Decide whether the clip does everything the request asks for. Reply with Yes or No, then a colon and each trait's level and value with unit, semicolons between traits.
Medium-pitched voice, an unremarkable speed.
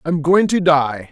No: medium, 160 Hz; fast, 215 wpm